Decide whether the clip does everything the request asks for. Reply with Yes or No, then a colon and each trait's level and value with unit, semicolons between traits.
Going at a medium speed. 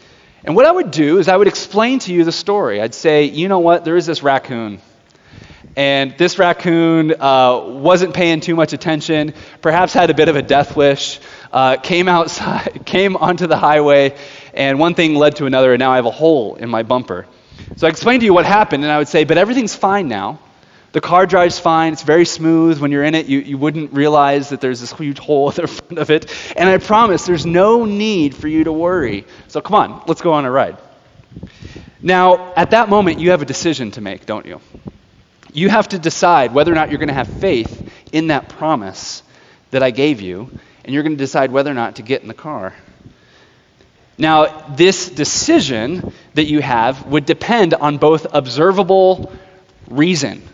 No: fast, 210 wpm